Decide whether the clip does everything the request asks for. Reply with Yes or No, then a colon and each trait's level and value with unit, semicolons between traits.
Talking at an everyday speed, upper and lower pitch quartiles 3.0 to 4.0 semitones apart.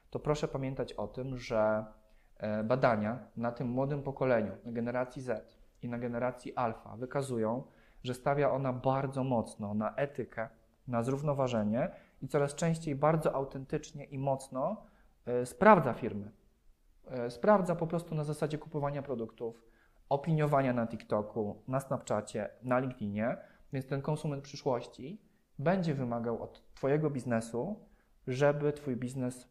Yes: average, 130 wpm; average, 3.7 semitones